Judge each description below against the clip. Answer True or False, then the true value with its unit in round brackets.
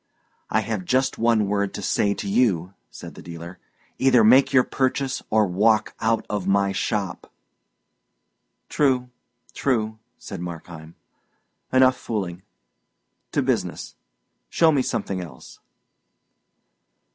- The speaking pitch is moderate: False (105 Hz)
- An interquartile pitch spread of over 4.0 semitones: True (5.3 semitones)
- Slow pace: True (120 wpm)